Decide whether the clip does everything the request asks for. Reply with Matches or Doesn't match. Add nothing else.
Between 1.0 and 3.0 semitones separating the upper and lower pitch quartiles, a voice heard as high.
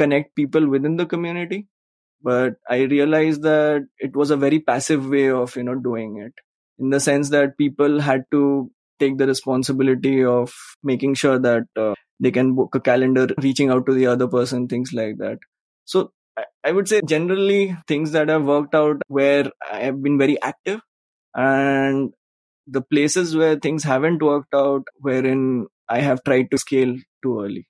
Doesn't match